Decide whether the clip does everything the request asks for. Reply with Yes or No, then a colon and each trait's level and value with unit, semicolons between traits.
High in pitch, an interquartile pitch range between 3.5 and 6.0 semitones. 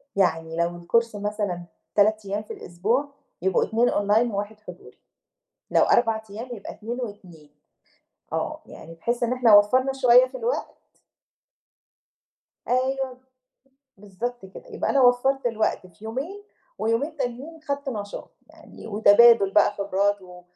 Yes: high, 220 Hz; average, 3.8 semitones